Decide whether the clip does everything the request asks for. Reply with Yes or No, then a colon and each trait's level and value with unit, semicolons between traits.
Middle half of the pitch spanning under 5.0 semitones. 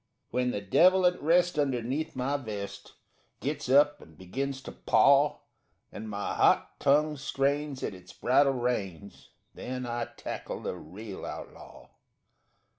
No: wide, 5.6 semitones